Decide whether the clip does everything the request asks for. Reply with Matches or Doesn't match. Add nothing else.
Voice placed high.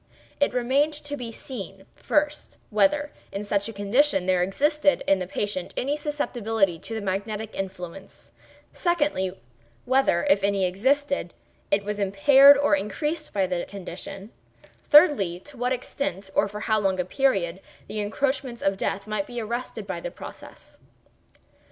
Matches